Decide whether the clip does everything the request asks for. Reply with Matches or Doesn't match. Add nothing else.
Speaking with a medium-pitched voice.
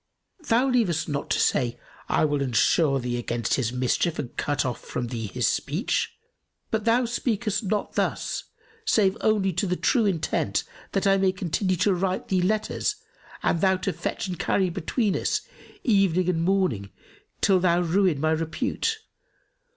Matches